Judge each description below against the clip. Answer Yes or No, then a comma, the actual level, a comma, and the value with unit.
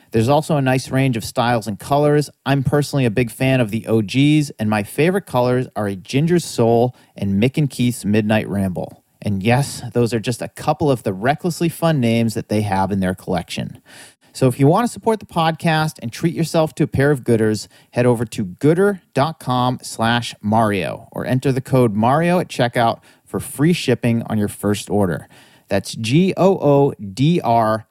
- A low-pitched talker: Yes, low, 125 Hz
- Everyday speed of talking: Yes, average, 185 wpm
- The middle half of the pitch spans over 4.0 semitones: Yes, average, 4.7 semitones